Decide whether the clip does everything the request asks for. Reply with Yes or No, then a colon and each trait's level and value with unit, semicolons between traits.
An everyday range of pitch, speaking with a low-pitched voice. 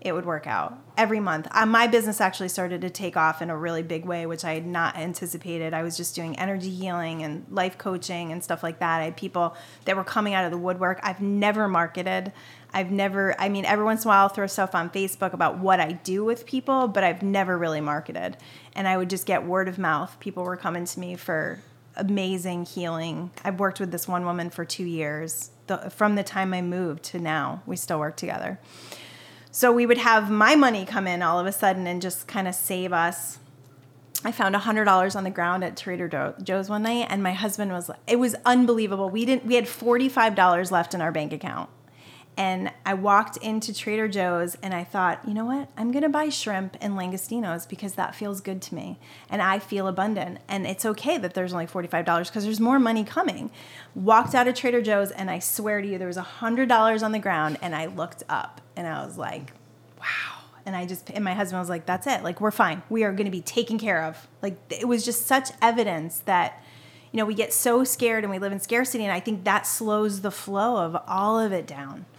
No: average, 3.6 semitones; high, 190 Hz